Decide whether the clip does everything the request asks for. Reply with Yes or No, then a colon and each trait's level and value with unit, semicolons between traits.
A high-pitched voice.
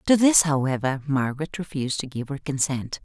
No: medium, 145 Hz